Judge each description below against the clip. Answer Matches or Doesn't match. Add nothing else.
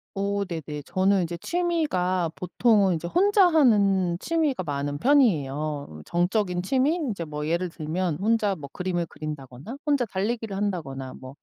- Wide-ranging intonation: Matches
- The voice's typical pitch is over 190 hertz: Doesn't match